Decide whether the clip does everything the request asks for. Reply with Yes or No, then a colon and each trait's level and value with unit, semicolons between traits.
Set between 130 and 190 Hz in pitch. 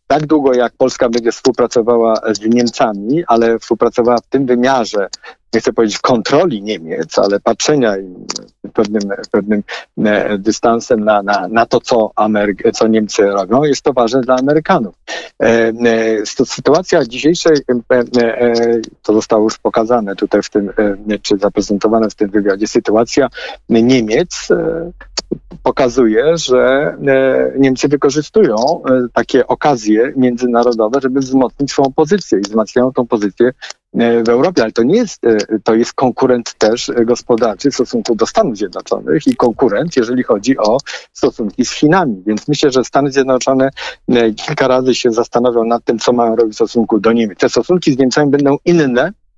No: low, 120 Hz